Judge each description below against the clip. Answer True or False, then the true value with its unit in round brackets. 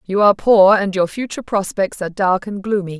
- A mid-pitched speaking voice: False (195 Hz)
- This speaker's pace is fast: True (220 wpm)